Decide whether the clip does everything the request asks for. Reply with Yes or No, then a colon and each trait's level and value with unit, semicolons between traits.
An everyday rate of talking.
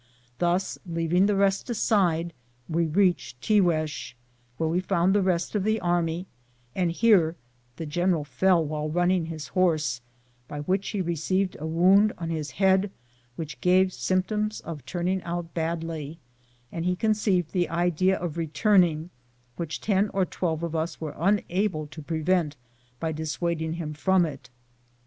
Yes: average, 150 wpm